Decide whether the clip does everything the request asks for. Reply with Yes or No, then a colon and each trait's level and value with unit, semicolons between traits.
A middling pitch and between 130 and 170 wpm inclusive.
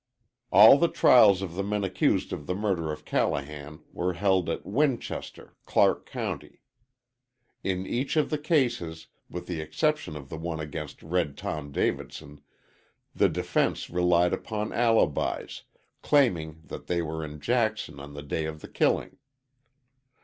No: very low, 90 Hz; average, 150 wpm